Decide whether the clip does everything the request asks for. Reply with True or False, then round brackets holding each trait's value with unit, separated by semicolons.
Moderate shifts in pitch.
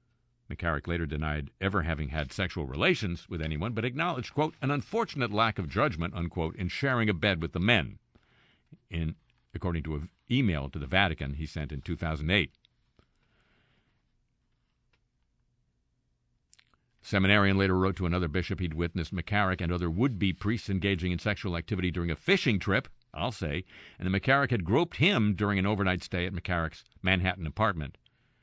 True (4.5 semitones)